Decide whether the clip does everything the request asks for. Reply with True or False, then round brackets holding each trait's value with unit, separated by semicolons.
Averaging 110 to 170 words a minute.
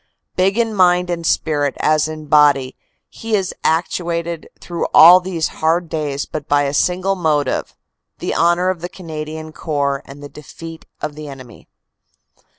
True (155 wpm)